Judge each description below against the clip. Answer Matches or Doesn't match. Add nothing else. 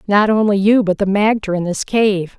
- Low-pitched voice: Doesn't match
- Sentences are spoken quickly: Matches